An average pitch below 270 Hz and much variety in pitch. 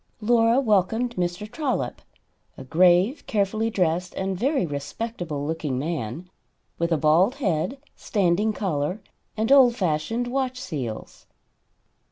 Yes: medium, 185 Hz; wide, 6.2 semitones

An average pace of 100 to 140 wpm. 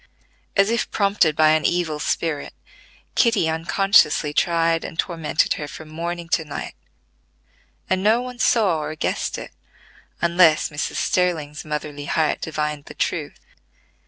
Yes: slow, 135 wpm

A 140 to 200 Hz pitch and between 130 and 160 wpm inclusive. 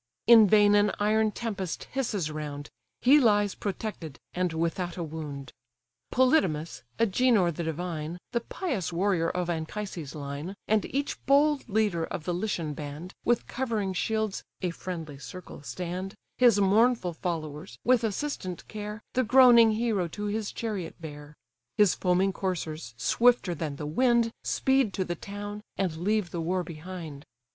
Yes: medium, 185 Hz; average, 150 wpm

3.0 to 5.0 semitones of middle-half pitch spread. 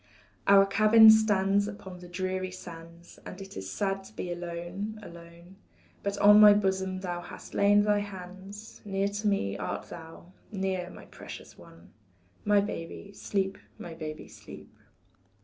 No: narrow, 2.6 semitones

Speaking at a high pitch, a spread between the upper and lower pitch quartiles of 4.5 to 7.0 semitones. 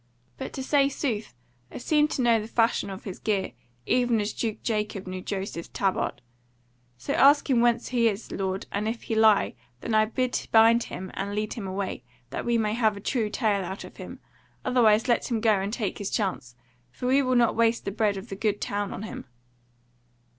No: high, 220 Hz; average, 3.0 semitones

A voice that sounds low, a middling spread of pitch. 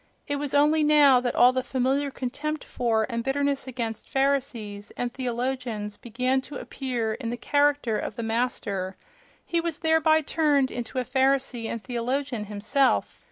No: very high, 255 Hz; average, 3.4 semitones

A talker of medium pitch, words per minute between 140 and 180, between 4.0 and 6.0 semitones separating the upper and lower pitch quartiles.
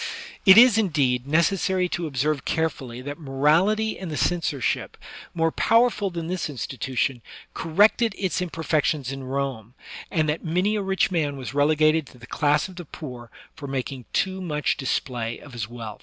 Yes: medium, 155 Hz; average, 165 wpm; average, 5.3 semitones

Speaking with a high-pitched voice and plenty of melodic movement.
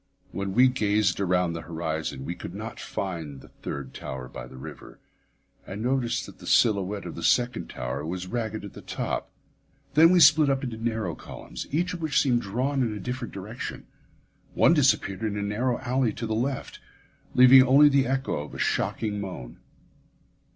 No: low, 110 Hz; wide, 5.9 semitones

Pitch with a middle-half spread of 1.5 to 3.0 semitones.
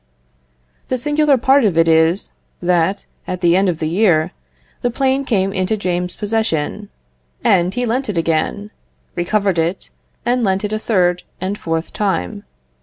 No: average, 4.3 semitones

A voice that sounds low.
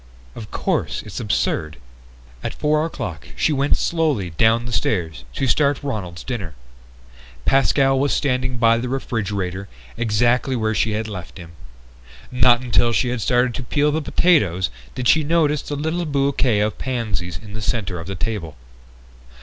Yes: low, 120 Hz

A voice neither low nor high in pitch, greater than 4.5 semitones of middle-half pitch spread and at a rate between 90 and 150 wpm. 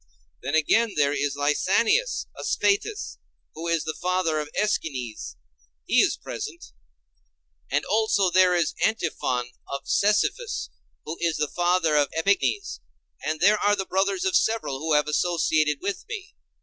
Yes: medium, 170 Hz; average, 5.3 semitones; average, 145 wpm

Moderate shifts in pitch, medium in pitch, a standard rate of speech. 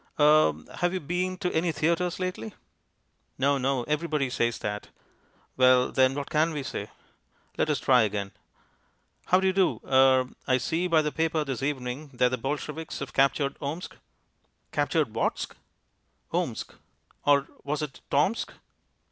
Yes: average, 3.8 semitones; medium, 145 Hz; average, 150 wpm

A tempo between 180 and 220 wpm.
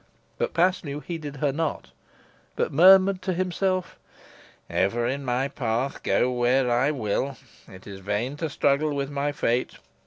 No: average, 150 wpm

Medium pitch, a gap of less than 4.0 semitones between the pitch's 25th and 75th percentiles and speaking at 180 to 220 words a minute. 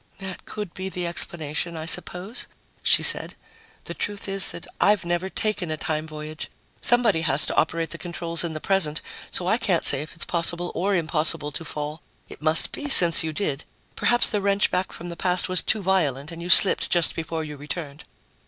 Yes: medium, 170 Hz; average, 3.4 semitones; average, 200 wpm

